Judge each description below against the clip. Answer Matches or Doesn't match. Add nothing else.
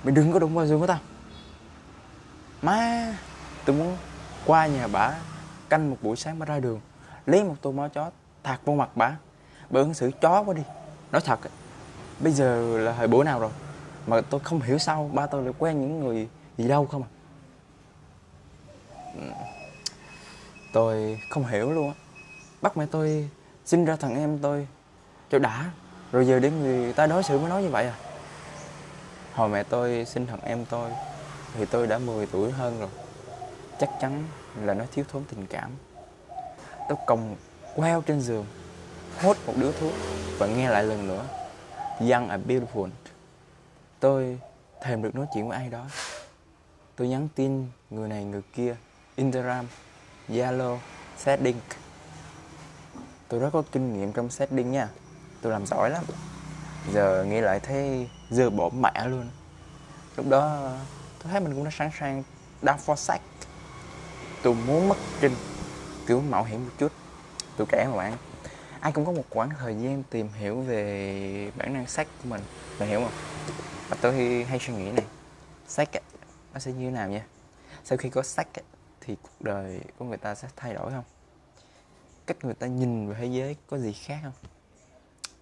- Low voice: Matches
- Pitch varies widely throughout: Doesn't match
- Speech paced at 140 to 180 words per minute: Matches